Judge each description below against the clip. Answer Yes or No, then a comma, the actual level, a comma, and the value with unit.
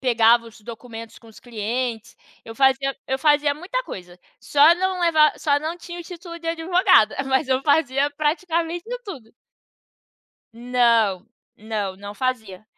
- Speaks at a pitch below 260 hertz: No, very high, 265 Hz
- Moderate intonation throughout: No, wide, 6.2 semitones